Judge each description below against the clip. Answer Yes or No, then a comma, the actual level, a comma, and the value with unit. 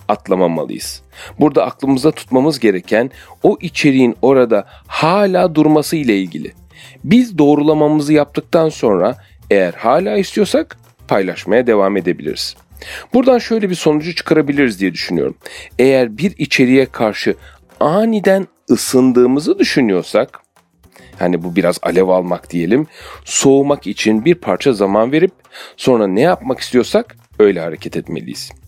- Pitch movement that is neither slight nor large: No, wide, 6.3 semitones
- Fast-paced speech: No, average, 115 wpm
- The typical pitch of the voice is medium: Yes, medium, 145 Hz